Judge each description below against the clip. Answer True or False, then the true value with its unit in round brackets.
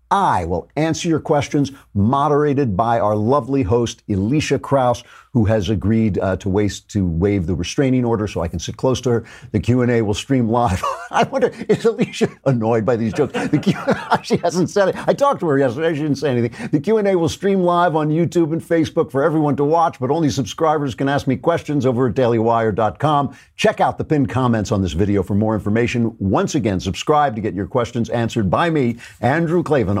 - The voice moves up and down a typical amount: False (5.8 semitones)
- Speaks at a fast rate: True (210 wpm)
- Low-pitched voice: True (130 Hz)